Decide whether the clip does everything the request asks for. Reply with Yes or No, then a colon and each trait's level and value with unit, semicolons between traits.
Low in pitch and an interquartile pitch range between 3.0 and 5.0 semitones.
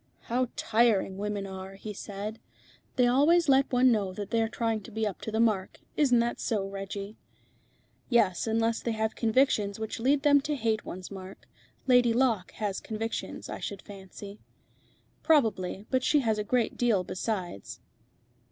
No: high, 220 Hz; average, 3.5 semitones